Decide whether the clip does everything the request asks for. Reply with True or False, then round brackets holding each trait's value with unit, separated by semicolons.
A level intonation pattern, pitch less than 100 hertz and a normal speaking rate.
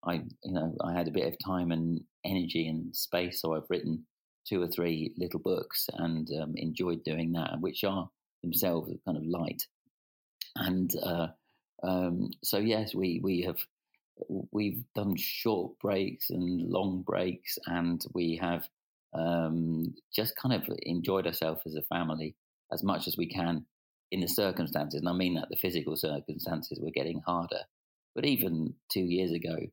True (1.9 semitones; 85 Hz; 165 wpm)